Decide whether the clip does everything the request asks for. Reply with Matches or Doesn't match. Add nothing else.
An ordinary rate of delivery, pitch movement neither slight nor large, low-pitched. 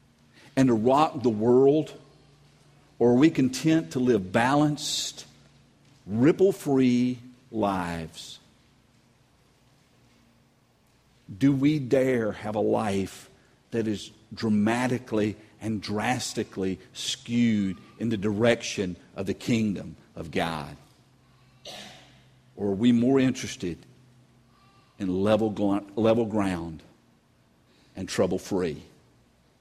Doesn't match